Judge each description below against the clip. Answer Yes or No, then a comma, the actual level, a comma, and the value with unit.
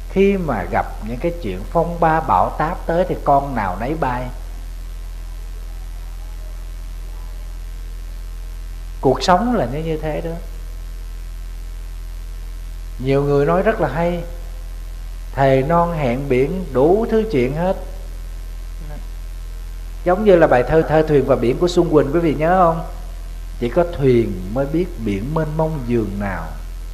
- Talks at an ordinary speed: No, slow, 140 wpm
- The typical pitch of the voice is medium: No, low, 110 Hz